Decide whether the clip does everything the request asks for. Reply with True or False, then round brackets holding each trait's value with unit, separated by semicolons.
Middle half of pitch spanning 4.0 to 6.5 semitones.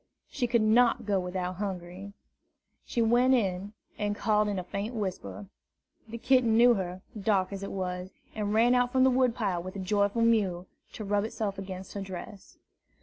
False (3.5 semitones)